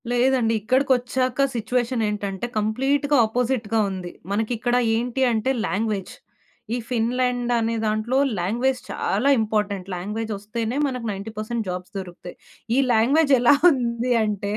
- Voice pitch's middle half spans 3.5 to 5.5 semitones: No, average, 2.9 semitones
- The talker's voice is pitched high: Yes, high, 230 Hz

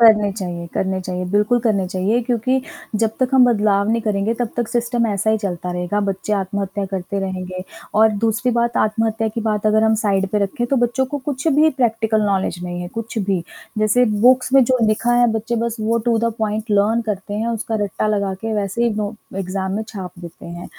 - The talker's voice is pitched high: Yes, high, 215 Hz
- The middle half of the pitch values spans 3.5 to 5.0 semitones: No, average, 3.0 semitones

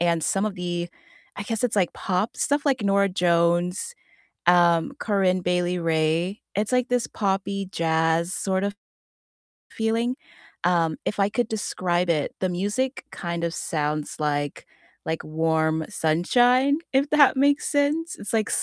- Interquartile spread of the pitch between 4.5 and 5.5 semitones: Yes, average, 4.8 semitones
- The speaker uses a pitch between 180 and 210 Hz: Yes, medium, 185 Hz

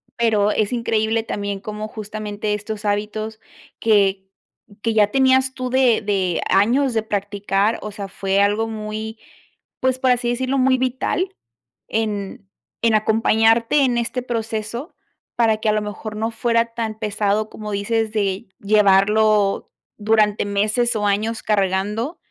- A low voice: No, high, 215 Hz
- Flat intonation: Yes, narrow, 2.1 semitones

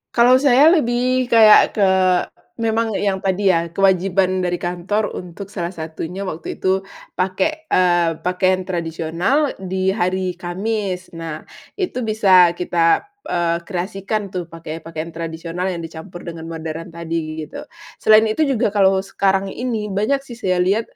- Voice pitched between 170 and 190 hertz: Yes, medium, 185 Hz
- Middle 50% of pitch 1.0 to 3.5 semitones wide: No, average, 3.9 semitones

